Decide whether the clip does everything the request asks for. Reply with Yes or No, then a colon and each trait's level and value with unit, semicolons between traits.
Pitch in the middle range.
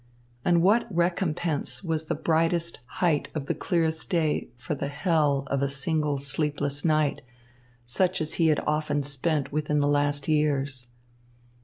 Yes: medium, 150 Hz